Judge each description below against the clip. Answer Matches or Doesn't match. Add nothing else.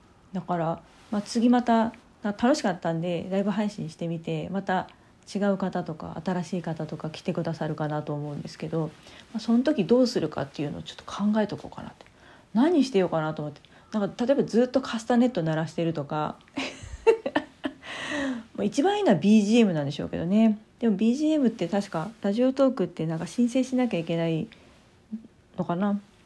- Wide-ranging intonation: Matches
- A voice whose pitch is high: Matches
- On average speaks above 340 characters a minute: Matches